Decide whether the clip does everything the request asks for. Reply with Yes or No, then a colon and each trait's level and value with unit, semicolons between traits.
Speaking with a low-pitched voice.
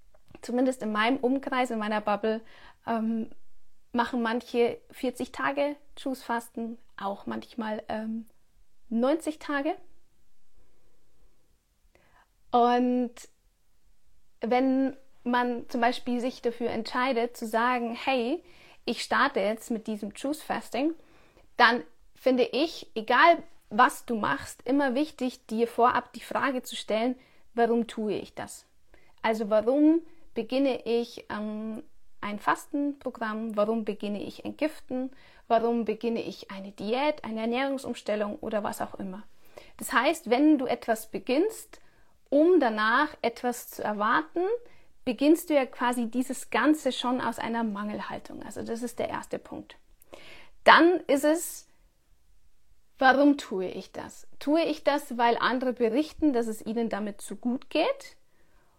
No: high, 245 Hz